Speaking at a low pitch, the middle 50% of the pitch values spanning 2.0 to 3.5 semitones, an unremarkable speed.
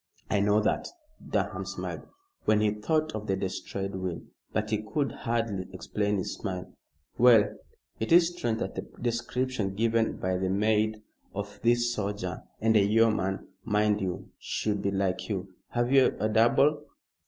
Yes: low, 105 Hz; average, 2.9 semitones; average, 160 wpm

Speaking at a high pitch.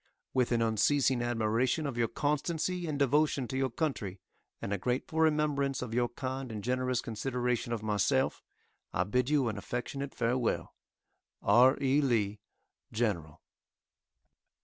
No: low, 125 Hz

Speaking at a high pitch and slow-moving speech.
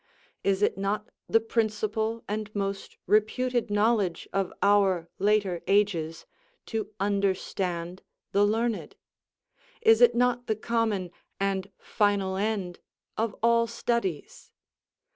Yes: high, 205 Hz; slow, 110 wpm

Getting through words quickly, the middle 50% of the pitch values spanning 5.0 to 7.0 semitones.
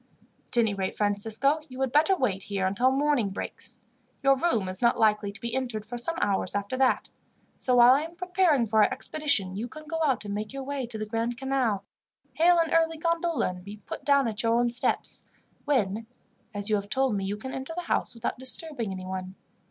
Yes: fast, 215 wpm; wide, 5.4 semitones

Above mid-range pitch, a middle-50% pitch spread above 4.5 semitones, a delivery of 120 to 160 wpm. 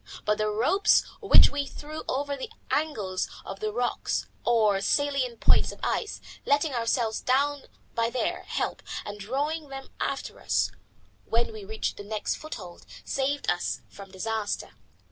Yes: high, 240 Hz; average, 5.2 semitones; average, 150 wpm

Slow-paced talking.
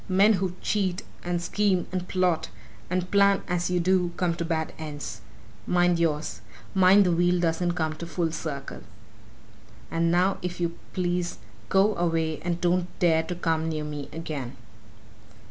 No: average, 155 wpm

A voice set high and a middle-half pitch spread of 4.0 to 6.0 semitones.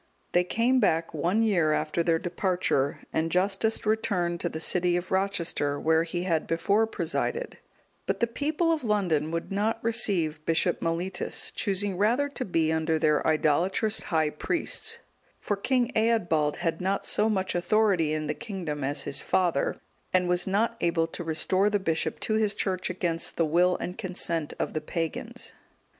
No: medium, 180 Hz; average, 4.4 semitones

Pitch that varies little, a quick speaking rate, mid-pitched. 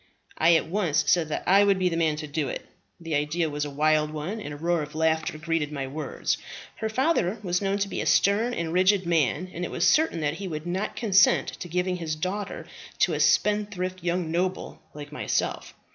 No: average, 3.6 semitones; fast, 220 wpm; medium, 170 Hz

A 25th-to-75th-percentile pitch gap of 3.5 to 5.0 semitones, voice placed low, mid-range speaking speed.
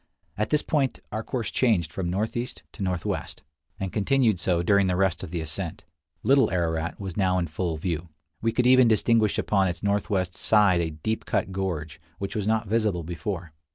Yes: average, 4.1 semitones; very low, 95 Hz; average, 190 wpm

